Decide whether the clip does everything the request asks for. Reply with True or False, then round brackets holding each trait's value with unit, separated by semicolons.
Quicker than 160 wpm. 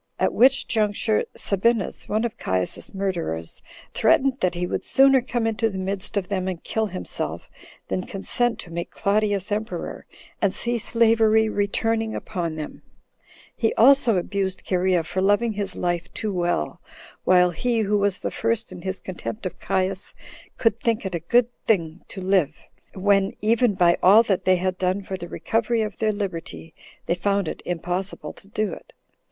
True (170 wpm)